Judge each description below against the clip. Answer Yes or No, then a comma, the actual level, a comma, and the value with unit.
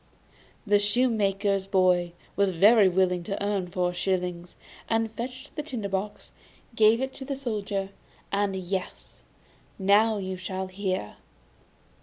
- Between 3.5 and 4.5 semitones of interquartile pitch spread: No, average, 2.7 semitones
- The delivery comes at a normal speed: No, slow, 130 wpm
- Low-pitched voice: No, high, 200 Hz